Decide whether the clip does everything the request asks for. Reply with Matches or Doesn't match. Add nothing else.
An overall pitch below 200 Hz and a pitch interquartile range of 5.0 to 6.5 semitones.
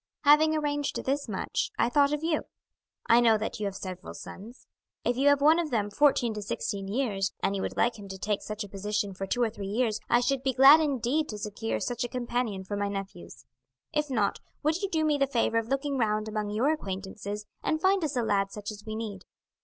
Doesn't match